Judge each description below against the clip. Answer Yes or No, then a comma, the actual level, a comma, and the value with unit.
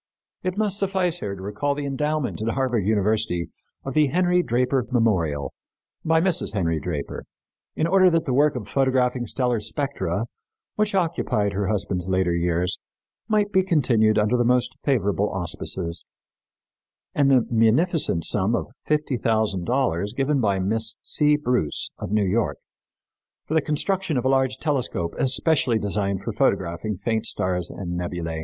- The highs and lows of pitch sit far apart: Yes, wide, 7.1 semitones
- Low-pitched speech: Yes, low, 120 Hz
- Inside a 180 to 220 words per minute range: No, average, 155 wpm